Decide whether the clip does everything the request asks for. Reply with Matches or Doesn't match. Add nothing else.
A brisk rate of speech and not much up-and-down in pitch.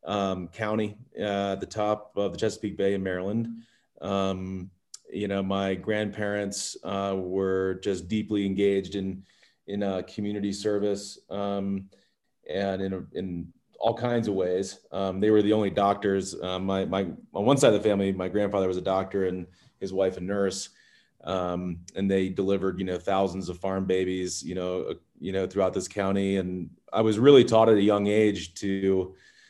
Doesn't match